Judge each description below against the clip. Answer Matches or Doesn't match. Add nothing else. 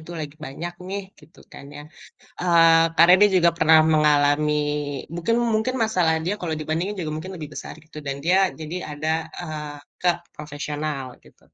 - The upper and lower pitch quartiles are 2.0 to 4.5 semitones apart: Matches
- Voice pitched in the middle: Matches